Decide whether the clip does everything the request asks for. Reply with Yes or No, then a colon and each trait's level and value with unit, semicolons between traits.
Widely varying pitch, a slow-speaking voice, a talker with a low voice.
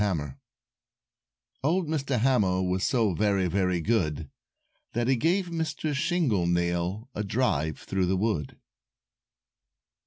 Yes: wide, 7.1 semitones; slow, 120 wpm; low, 105 Hz